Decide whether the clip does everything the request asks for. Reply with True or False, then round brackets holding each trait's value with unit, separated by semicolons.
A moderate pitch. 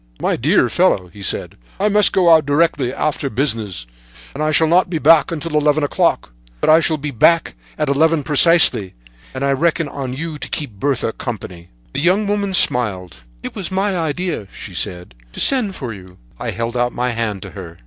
True (145 Hz)